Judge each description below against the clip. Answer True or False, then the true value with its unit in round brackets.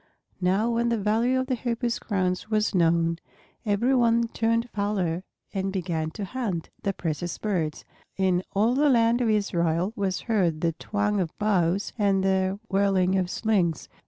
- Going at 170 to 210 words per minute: False (160 wpm)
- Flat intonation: False (4.0 semitones)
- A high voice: True (200 Hz)